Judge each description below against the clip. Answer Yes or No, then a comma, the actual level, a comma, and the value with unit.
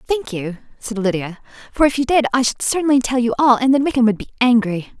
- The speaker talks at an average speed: No, fast, 240 wpm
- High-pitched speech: Yes, high, 245 Hz